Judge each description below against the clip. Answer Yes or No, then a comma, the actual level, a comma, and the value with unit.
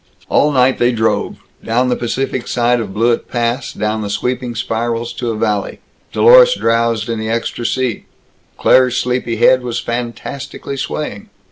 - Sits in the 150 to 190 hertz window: No, low, 120 Hz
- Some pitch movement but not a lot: No, narrow, 1.9 semitones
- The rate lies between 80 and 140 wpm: No, average, 155 wpm